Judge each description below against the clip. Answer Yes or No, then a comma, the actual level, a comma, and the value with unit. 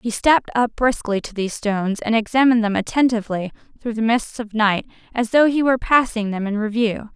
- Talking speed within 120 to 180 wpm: No, average, 200 wpm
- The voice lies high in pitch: Yes, high, 225 Hz